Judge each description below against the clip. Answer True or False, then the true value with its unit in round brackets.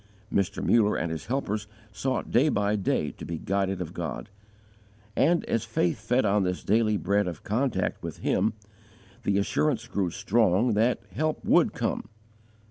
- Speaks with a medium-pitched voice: False (105 Hz)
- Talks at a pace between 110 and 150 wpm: False (160 wpm)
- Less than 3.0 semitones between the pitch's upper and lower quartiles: False (3.5 semitones)